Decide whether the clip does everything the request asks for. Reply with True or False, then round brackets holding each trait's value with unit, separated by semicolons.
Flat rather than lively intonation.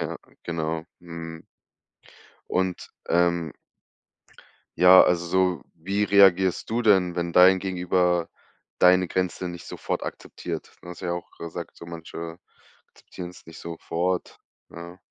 True (1.5 semitones)